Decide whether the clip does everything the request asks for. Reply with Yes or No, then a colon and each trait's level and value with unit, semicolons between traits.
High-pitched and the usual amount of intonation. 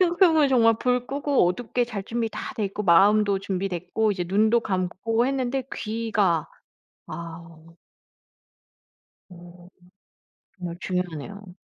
Yes: high, 205 Hz; average, 4.9 semitones